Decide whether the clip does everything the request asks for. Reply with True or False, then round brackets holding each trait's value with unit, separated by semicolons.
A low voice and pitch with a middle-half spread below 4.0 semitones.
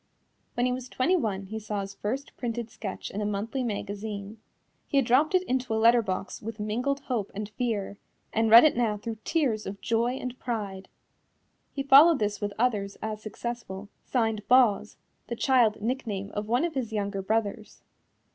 False (225 Hz; 3.3 semitones)